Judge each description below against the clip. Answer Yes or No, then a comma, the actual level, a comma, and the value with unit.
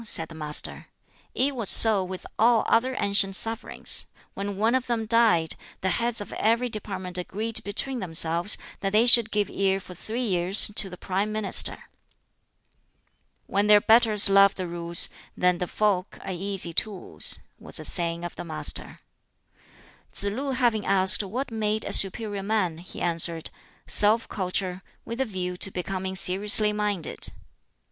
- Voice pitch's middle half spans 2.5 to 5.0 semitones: Yes, average, 3.3 semitones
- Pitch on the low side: No, high, 200 Hz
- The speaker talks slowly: No, average, 160 wpm